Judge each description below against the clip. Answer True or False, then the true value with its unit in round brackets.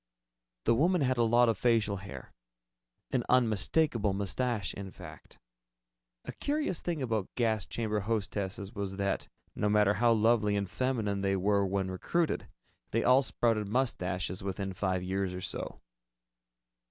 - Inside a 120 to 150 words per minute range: True (145 wpm)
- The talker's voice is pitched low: True (105 Hz)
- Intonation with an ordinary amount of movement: True (3.6 semitones)